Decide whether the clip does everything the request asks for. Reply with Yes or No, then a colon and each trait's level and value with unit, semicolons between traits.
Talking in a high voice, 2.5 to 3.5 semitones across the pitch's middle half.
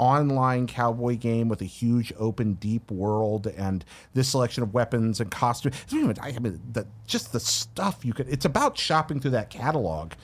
No: low, 120 Hz; average, 2.9 semitones